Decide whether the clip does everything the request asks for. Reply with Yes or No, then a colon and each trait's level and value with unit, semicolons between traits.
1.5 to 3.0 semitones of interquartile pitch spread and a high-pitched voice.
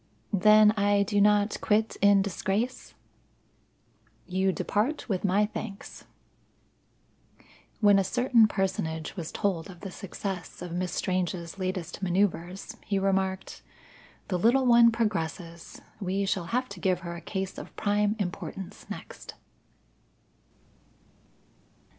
Yes: narrow, 2.4 semitones; high, 195 Hz